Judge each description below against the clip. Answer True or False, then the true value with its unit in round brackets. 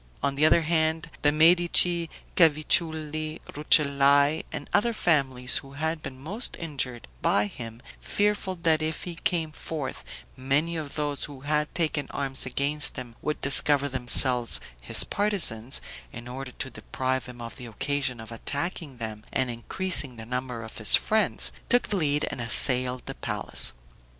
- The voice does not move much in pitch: False (3.9 semitones)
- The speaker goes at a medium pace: True (155 wpm)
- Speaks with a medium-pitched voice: True (145 Hz)